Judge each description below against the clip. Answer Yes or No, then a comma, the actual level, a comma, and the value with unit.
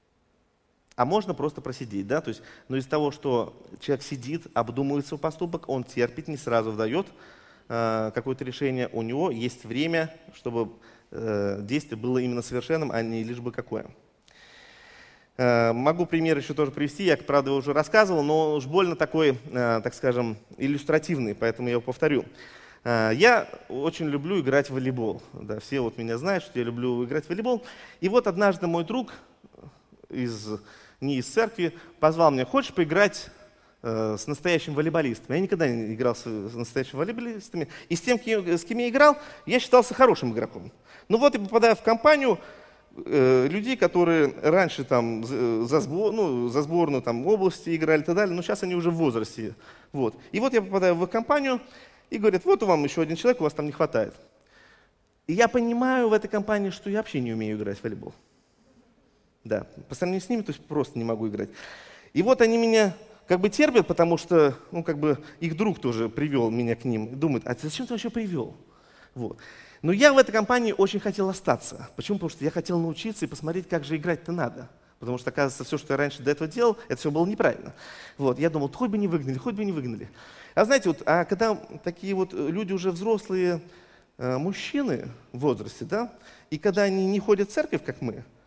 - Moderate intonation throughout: No, wide, 7.7 semitones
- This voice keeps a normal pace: No, fast, 190 wpm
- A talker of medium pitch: Yes, medium, 160 Hz